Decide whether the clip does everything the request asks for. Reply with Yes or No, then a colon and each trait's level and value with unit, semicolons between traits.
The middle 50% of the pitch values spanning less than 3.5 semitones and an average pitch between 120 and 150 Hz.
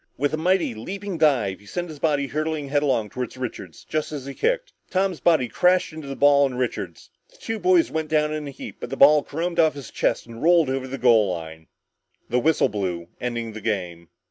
No: wide, 5.4 semitones; medium, 140 Hz